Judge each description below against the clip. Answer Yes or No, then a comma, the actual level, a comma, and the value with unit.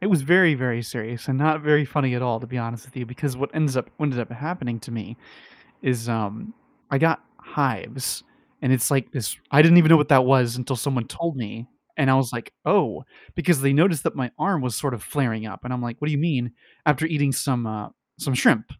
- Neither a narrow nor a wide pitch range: Yes, average, 3.7 semitones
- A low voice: Yes, low, 130 Hz